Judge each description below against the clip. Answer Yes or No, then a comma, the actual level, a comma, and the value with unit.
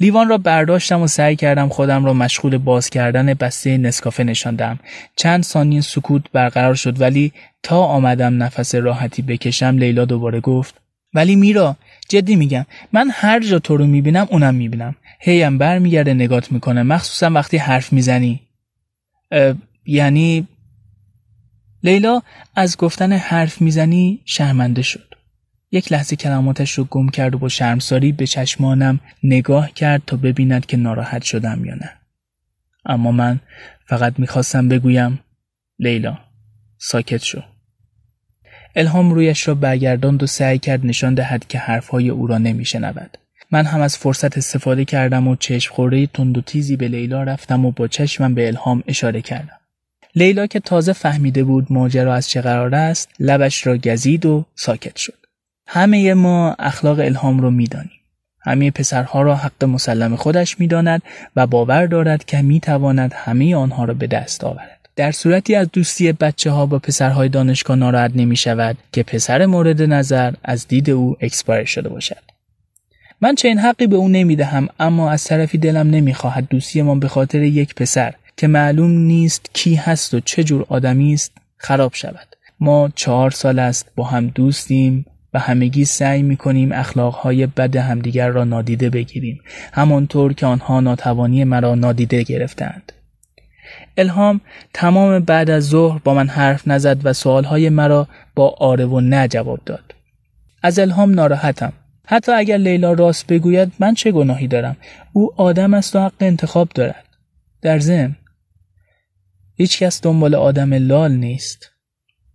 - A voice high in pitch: No, low, 135 Hz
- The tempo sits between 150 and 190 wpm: Yes, fast, 155 wpm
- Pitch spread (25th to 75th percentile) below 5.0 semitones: Yes, average, 4.1 semitones